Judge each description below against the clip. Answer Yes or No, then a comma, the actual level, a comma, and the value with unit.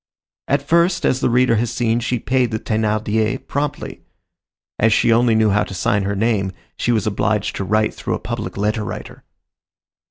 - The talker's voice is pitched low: Yes, low, 110 Hz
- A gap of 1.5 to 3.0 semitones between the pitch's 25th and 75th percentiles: Yes, narrow, 2.4 semitones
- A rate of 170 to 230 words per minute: Yes, average, 185 wpm